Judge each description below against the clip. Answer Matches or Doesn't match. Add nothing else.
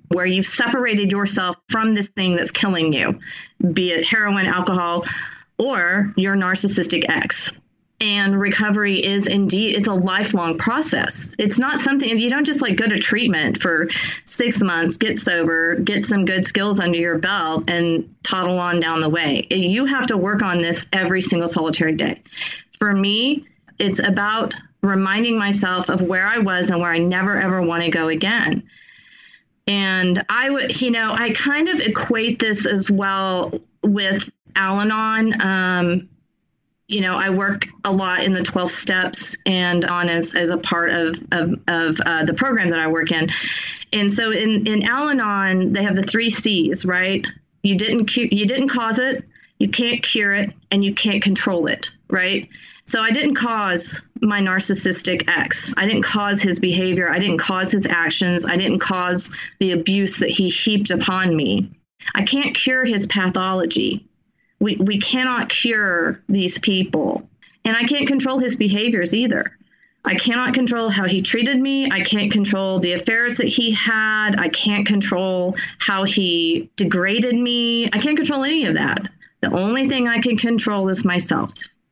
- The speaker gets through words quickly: Doesn't match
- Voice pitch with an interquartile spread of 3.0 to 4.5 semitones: Matches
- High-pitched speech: Matches